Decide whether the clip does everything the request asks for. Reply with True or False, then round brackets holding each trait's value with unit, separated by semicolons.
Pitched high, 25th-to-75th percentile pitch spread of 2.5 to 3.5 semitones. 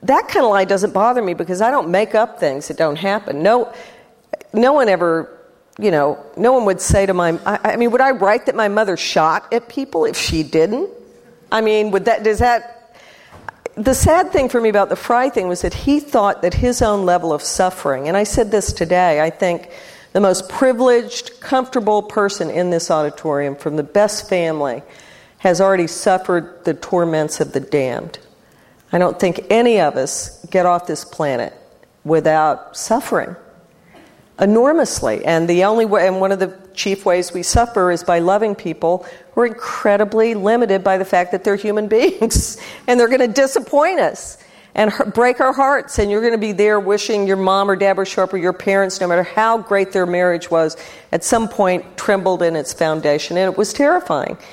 False (200 Hz; 4.7 semitones)